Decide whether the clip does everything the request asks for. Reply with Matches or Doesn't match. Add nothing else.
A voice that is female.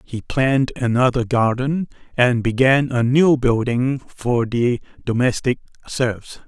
Doesn't match